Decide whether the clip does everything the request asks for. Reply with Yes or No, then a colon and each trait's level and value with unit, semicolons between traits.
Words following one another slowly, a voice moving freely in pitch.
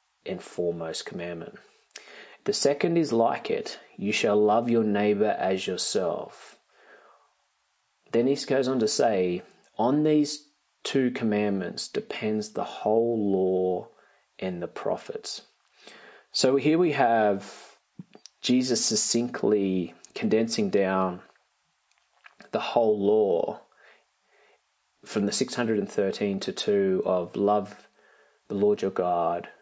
No: slow, 110 wpm; average, 4.9 semitones